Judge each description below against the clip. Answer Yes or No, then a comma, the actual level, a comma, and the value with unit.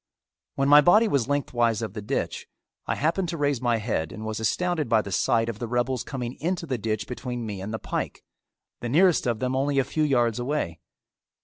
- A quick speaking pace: Yes, fast, 215 wpm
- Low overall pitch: Yes, low, 125 Hz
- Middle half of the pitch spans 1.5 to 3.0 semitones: No, average, 4.4 semitones